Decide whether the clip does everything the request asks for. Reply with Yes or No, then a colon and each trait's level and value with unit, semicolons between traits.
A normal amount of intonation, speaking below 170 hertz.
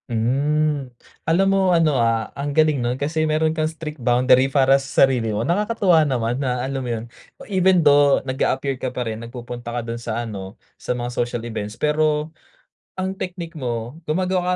Yes: average, 4.6 semitones; low, 135 Hz